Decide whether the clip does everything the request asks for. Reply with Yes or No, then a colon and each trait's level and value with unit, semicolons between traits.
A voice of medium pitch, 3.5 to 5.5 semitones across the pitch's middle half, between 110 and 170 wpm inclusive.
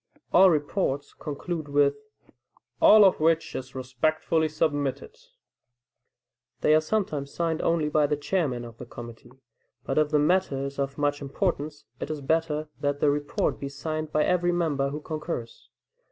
No: medium, 150 Hz; narrow, 2.6 semitones; average, 155 wpm